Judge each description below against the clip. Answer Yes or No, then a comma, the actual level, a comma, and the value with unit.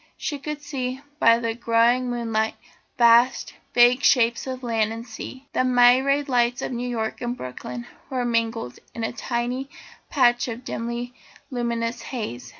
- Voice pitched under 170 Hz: No, high, 240 Hz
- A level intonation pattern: Yes, narrow, 1.6 semitones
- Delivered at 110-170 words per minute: Yes, average, 150 wpm